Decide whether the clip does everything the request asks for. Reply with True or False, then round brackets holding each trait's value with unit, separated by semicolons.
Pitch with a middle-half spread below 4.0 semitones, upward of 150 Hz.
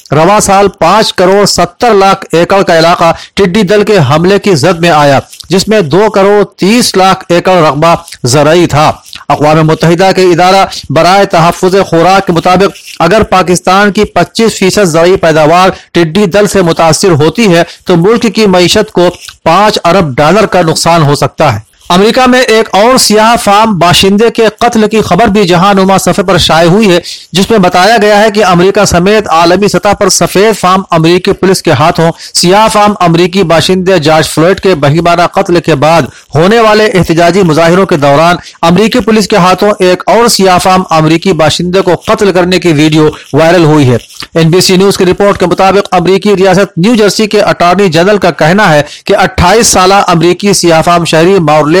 True (3.2 semitones; 185 Hz)